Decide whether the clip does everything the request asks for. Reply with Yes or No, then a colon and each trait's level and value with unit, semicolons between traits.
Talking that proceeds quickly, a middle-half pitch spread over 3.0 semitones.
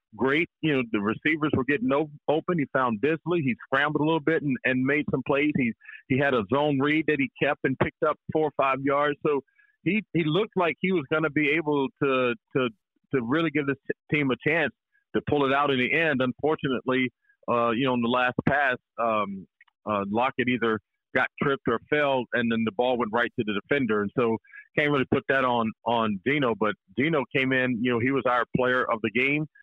Yes: fast, 225 wpm; average, 3.5 semitones